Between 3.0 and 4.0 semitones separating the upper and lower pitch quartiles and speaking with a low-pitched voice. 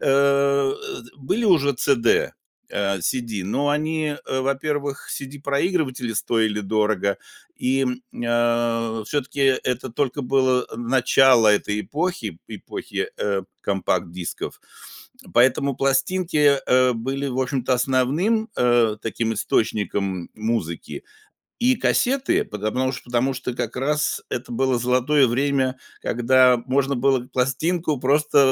Yes: average, 3.3 semitones; low, 130 Hz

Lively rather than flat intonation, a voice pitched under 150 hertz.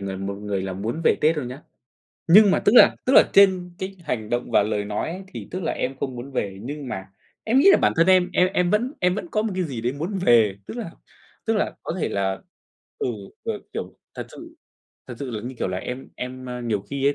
Yes: wide, 8.8 semitones; low, 135 Hz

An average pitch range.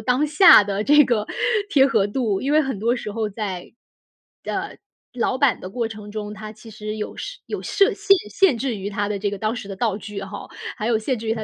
Yes: average, 3.5 semitones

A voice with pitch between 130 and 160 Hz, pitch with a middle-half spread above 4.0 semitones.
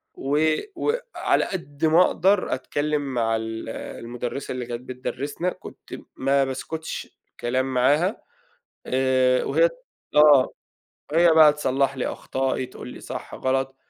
No: low, 135 Hz; average, 3.5 semitones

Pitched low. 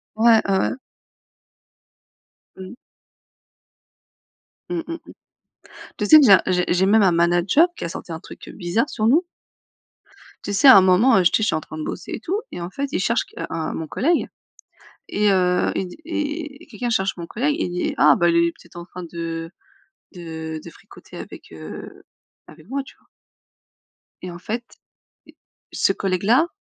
No: high, 190 Hz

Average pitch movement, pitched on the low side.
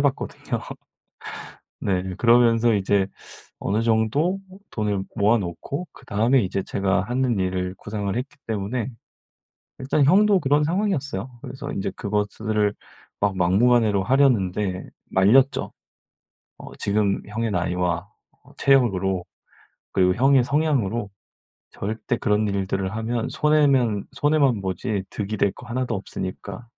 Yes: average, 5.0 semitones; low, 110 Hz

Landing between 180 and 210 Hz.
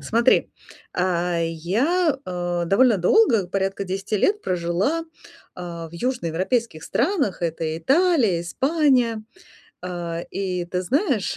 Yes: high, 190 Hz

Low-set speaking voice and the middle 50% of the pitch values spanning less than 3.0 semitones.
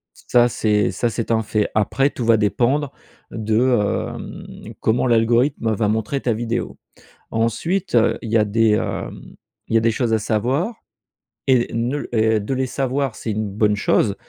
Yes: low, 115 Hz; narrow, 2.6 semitones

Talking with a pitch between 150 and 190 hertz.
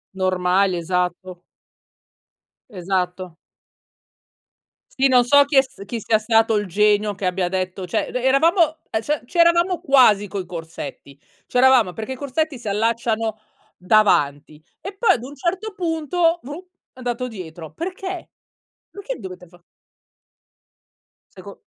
No: high, 220 Hz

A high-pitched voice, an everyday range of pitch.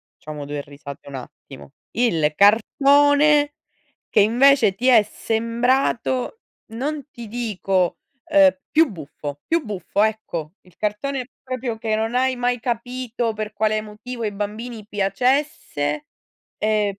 Yes: high, 225 Hz; average, 4.2 semitones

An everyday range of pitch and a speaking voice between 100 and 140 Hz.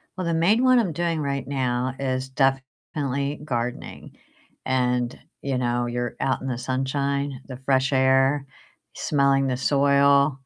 No: narrow, 1.5 semitones; low, 135 Hz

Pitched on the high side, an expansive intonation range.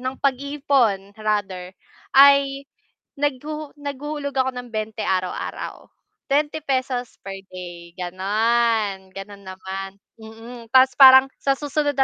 Yes: high, 245 Hz; wide, 5.9 semitones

